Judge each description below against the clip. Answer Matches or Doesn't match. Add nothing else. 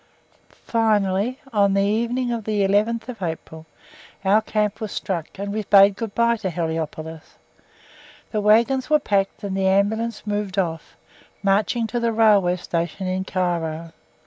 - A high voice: Matches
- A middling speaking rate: Matches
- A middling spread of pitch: Matches